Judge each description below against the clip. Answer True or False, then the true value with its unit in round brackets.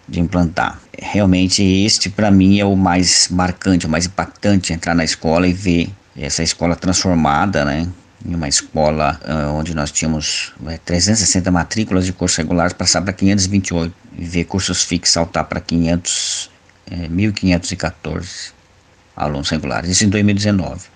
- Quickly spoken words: False (140 wpm)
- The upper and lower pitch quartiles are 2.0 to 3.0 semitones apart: True (2.5 semitones)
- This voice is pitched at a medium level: False (90 Hz)